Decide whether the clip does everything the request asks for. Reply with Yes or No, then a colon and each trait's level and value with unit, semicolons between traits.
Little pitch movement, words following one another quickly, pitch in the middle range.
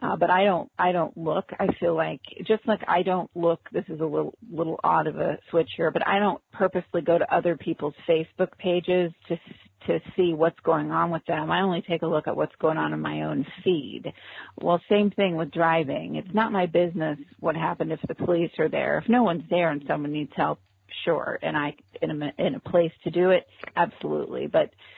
Yes: narrow, 2.2 semitones; fast, 225 wpm; medium, 170 Hz